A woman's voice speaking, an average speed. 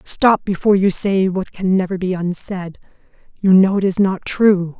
Yes: female; average, 190 wpm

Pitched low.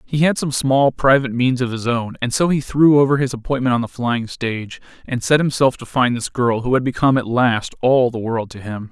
Yes: low, 125 Hz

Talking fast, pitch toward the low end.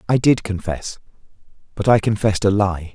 No: average, 165 wpm; low, 100 Hz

